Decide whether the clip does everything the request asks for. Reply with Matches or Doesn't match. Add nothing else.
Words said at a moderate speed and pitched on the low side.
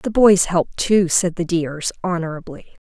Doesn't match